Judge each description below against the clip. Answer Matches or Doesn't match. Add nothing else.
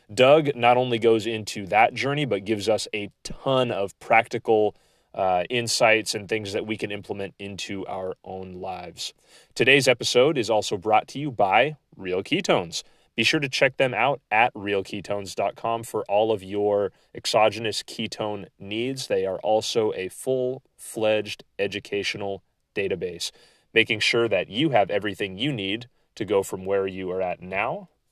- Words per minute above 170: Doesn't match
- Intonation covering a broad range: Doesn't match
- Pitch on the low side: Matches